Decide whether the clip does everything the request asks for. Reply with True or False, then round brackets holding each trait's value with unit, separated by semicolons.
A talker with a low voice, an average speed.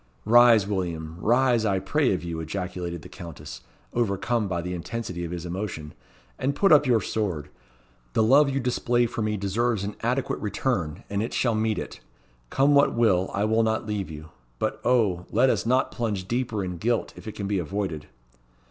True (105 Hz; 190 wpm)